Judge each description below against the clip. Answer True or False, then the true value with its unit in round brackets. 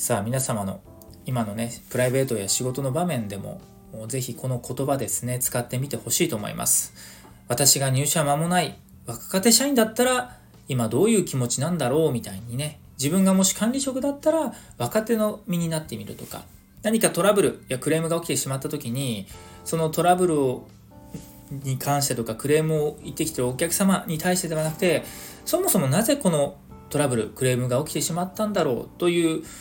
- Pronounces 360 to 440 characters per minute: True (385 characters per minute)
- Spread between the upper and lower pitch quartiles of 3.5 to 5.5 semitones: False (6.5 semitones)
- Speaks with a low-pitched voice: False (145 Hz)